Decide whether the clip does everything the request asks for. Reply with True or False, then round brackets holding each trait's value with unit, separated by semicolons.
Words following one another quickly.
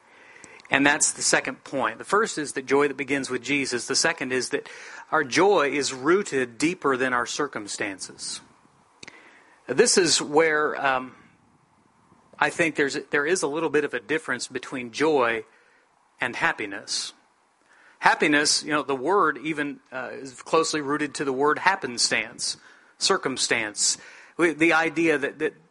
False (150 wpm)